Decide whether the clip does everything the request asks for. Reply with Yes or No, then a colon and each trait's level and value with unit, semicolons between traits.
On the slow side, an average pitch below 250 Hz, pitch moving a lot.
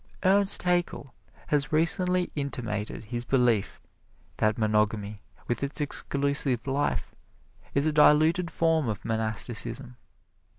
Yes: slow, 110 wpm; medium, 140 Hz; wide, 5.8 semitones